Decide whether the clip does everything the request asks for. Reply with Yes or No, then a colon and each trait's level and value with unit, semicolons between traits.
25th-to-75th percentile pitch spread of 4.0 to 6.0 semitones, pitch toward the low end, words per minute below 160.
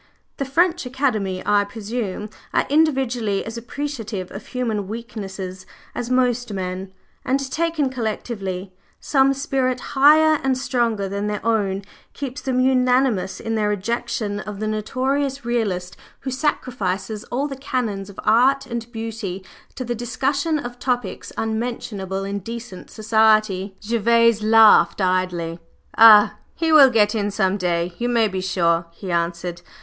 No: average, 4.5 semitones; high, 225 Hz; average, 140 wpm